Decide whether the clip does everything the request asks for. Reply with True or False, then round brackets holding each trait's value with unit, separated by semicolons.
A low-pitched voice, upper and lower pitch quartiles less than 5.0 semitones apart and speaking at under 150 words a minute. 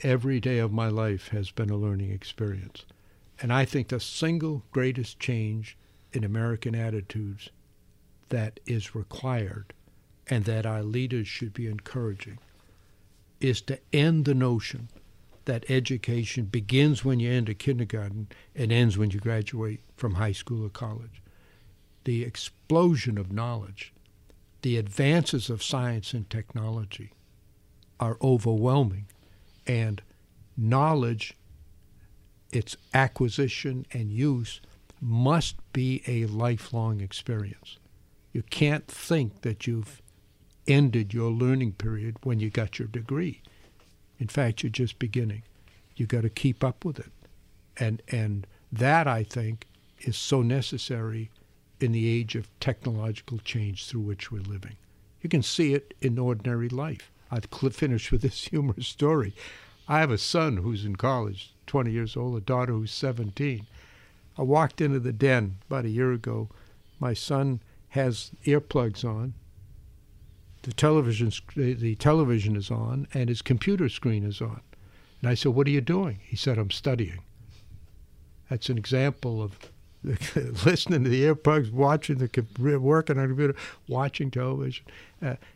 True (115 Hz; 4.1 semitones; 140 wpm)